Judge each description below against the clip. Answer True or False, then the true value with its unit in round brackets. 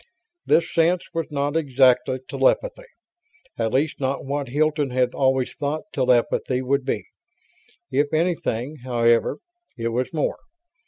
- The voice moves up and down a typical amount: True (3.5 semitones)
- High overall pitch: False (140 Hz)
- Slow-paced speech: True (125 wpm)